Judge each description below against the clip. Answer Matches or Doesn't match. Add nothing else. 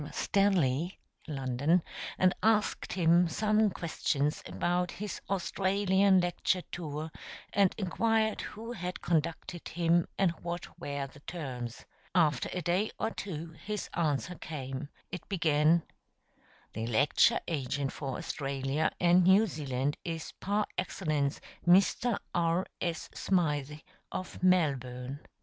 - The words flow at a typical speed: Doesn't match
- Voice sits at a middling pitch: Matches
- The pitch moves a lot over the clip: Doesn't match